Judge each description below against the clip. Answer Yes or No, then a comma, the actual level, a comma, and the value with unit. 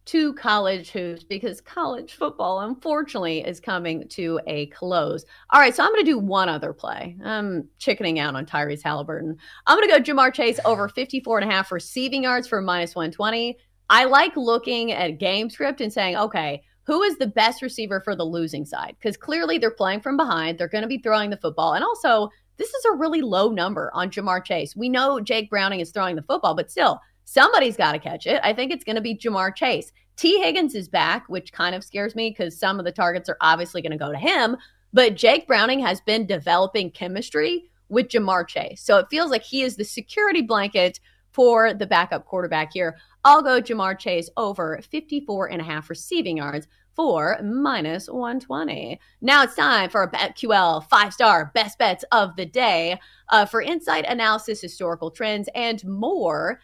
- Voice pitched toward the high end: Yes, high, 210 Hz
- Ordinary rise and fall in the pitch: No, wide, 5.8 semitones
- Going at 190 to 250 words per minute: Yes, average, 200 wpm